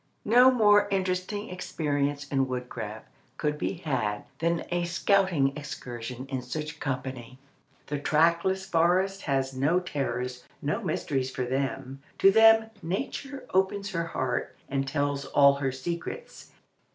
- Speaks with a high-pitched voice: No, medium, 150 Hz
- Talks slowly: Yes, slow, 130 wpm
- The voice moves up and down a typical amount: No, wide, 5.9 semitones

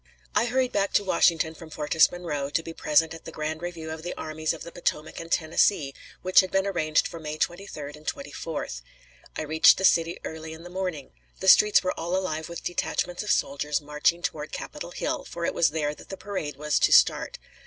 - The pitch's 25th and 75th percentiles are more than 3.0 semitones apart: No, average, 2.7 semitones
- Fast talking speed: Yes, fast, 215 wpm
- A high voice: No, medium, 165 Hz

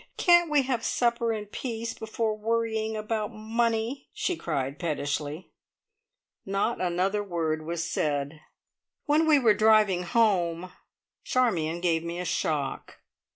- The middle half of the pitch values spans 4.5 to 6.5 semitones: Yes, wide, 5.4 semitones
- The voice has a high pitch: Yes, high, 210 Hz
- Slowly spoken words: Yes, slow, 125 wpm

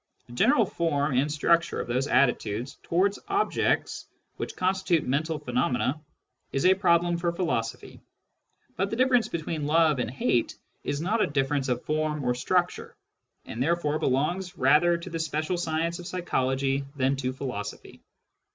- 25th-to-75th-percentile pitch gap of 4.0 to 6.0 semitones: Yes, average, 4.5 semitones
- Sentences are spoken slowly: No, average, 155 wpm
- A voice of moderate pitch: Yes, medium, 155 Hz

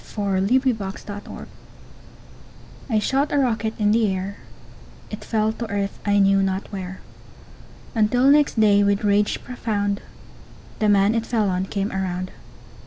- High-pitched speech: Yes, high, 205 Hz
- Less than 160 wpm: Yes, average, 150 wpm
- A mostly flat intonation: Yes, narrow, 2.2 semitones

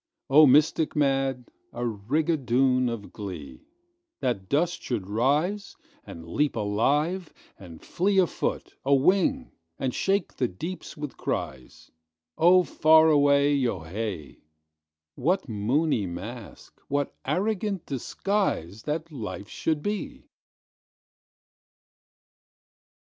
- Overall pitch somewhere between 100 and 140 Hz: Yes, low, 135 Hz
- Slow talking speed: Yes, slow, 90 wpm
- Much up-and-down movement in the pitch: Yes, wide, 8.2 semitones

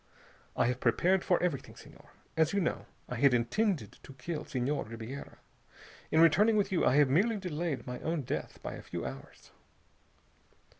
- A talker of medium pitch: Yes, medium, 150 Hz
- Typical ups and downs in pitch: No, wide, 6.0 semitones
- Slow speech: No, average, 170 wpm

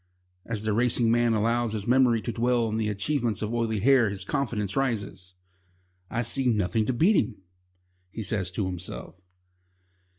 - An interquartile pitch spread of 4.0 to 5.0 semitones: No, average, 2.7 semitones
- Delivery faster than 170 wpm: No, average, 165 wpm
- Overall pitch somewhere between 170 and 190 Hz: No, low, 115 Hz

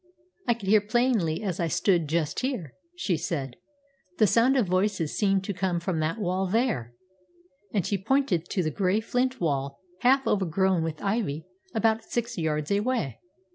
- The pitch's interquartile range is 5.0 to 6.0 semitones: Yes, wide, 5.4 semitones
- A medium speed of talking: Yes, average, 170 wpm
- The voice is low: No, high, 190 Hz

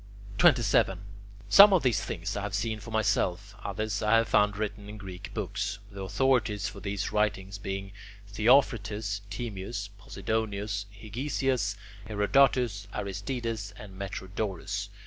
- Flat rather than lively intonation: Yes, narrow, 2.1 semitones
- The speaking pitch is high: No, low, 105 Hz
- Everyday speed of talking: No, slow, 125 wpm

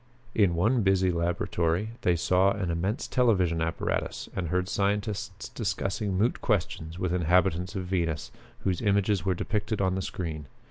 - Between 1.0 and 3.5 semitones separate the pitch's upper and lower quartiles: Yes, average, 2.9 semitones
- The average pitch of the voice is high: No, very low, 95 Hz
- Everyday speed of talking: Yes, average, 150 wpm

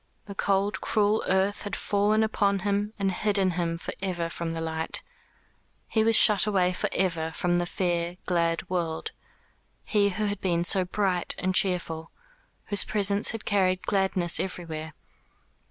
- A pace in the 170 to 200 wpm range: No, average, 155 wpm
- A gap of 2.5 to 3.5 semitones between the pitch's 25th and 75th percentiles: Yes, average, 2.8 semitones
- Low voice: No, high, 190 Hz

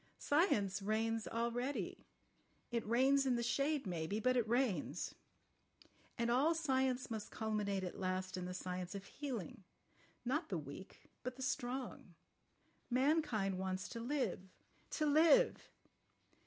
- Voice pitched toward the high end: Yes, high, 235 Hz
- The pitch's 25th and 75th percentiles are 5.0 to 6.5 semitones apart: Yes, wide, 5.4 semitones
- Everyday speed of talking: No, slow, 120 wpm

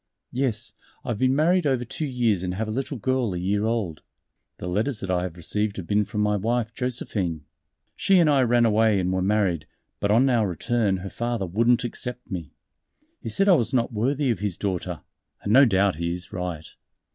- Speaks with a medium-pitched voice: No, low, 105 Hz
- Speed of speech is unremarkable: No, fast, 210 wpm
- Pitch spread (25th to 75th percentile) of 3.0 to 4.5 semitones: No, average, 4.9 semitones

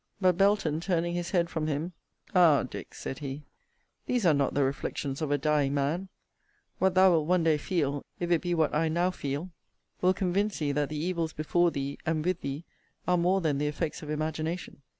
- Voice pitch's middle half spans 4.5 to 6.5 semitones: No, average, 3.4 semitones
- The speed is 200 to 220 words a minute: Yes, fast, 205 wpm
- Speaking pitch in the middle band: Yes, medium, 160 Hz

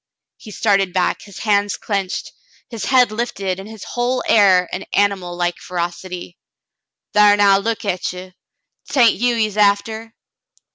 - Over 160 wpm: No, average, 145 wpm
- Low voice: No, high, 200 Hz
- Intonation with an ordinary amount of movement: Yes, average, 3.0 semitones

